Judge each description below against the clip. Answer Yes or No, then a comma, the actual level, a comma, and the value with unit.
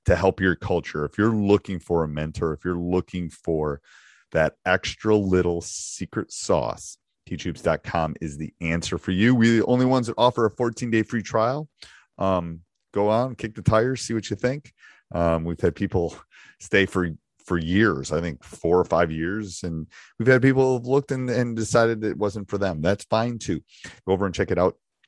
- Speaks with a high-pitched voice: No, low, 100 Hz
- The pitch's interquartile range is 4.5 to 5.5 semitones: Yes, average, 5.1 semitones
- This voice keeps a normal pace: Yes, average, 195 wpm